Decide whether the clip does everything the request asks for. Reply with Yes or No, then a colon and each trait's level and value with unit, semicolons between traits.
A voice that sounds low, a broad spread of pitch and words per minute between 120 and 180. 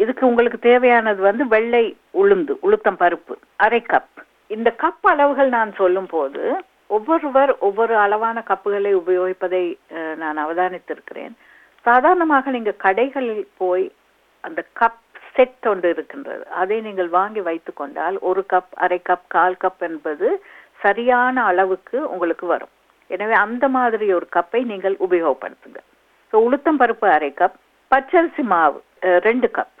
No: high, 215 Hz; wide, 5.8 semitones; average, 125 wpm